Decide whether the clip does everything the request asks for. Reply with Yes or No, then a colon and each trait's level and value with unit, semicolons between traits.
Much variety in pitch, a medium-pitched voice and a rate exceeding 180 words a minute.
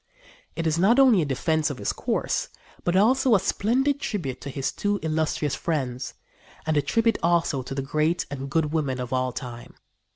Yes: wide, 6.0 semitones; medium, 155 Hz; average, 190 wpm